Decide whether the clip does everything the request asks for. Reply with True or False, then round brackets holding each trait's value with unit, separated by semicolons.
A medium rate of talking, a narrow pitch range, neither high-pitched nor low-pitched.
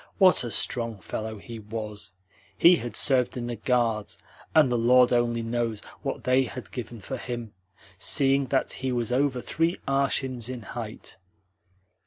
False (160 wpm; 2.2 semitones; 120 Hz)